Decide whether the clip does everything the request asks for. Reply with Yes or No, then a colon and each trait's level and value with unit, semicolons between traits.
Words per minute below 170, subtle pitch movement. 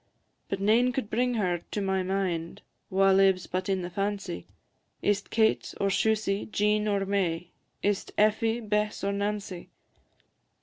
Yes: average, 160 wpm; narrow, 1.9 semitones